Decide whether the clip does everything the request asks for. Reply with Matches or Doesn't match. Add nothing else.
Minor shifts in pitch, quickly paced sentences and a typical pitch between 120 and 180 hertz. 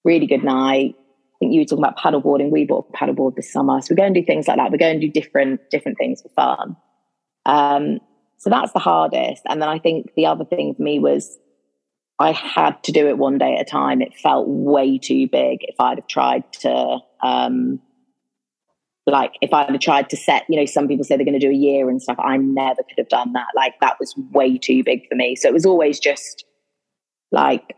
Doesn't match